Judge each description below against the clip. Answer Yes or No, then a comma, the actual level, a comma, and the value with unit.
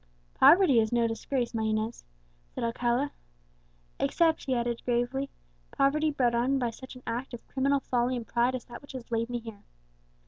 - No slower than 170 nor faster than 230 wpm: Yes, average, 180 wpm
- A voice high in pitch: Yes, high, 245 Hz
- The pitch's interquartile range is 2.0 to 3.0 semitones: Yes, narrow, 2.4 semitones